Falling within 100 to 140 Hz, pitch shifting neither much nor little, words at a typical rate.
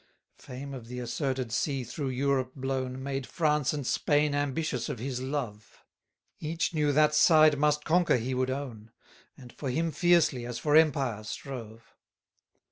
Yes: low, 135 Hz; average, 3.1 semitones; average, 160 wpm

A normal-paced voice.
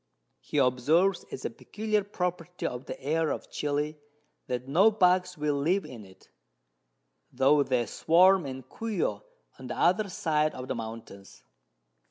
Yes: average, 150 wpm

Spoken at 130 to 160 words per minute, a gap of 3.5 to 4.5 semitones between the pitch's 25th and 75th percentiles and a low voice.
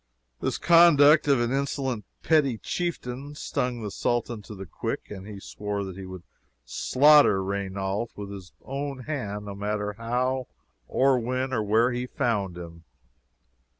No: average, 150 wpm; average, 4.9 semitones; low, 115 Hz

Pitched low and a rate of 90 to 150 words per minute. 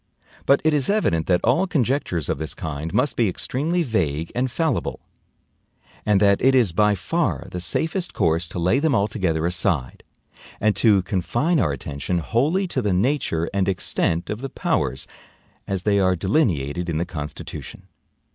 No: low, 100 Hz; average, 165 wpm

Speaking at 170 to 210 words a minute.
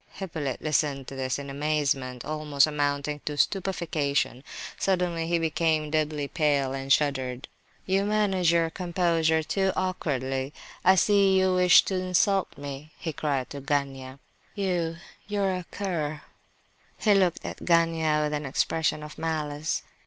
No: average, 140 wpm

